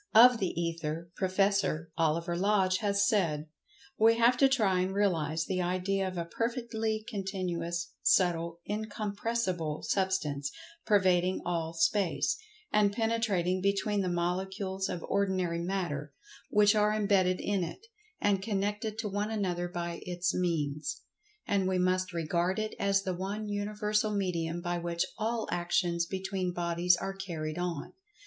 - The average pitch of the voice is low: No, medium, 185 Hz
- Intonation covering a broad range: No, average, 3.1 semitones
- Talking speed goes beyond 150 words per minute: No, average, 140 wpm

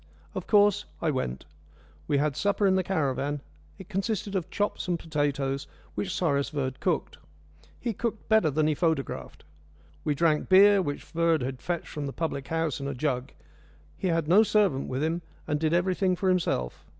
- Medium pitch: Yes, medium, 165 Hz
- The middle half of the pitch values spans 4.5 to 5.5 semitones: Yes, average, 5.0 semitones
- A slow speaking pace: No, average, 180 wpm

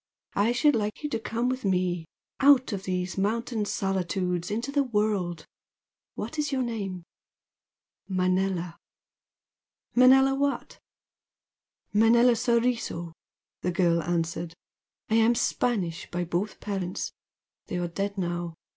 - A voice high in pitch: Yes, high, 200 Hz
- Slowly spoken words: Yes, slow, 120 wpm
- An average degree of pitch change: Yes, average, 5.0 semitones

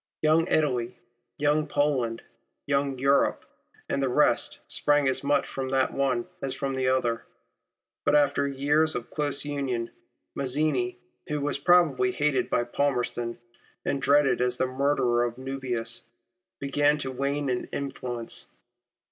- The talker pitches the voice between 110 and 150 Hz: Yes, low, 135 Hz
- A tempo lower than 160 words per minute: Yes, average, 140 wpm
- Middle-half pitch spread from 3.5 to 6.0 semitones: No, narrow, 2.6 semitones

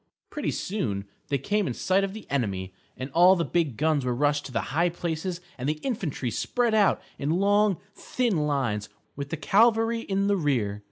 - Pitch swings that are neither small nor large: No, wide, 6.7 semitones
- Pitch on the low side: No, medium, 160 Hz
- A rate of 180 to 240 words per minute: Yes, average, 200 wpm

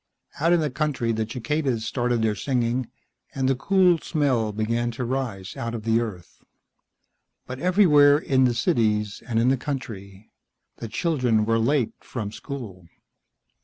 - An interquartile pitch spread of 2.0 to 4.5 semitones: Yes, average, 3.9 semitones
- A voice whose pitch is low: Yes, low, 120 Hz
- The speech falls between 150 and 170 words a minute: Yes, average, 155 wpm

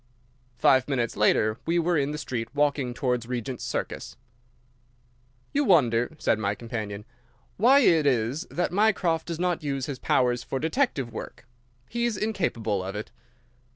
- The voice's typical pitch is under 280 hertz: Yes, low, 135 Hz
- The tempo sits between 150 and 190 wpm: Yes, average, 155 wpm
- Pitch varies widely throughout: Yes, wide, 6.5 semitones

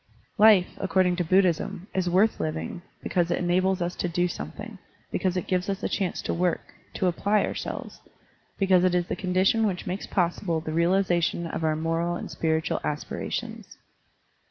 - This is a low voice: No, medium, 180 Hz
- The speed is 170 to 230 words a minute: Yes, average, 175 wpm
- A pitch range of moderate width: No, narrow, 1.8 semitones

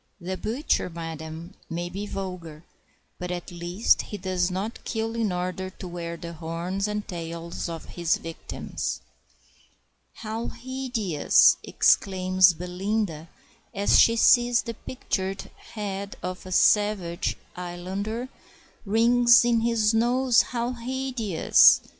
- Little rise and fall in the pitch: No, average, 4.5 semitones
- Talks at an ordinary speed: No, slow, 120 wpm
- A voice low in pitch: No, high, 190 Hz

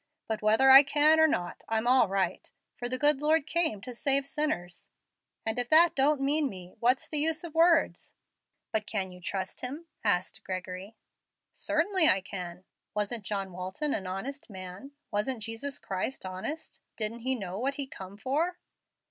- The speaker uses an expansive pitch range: Yes, wide, 7.0 semitones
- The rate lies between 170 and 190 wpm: Yes, average, 175 wpm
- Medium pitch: No, high, 240 Hz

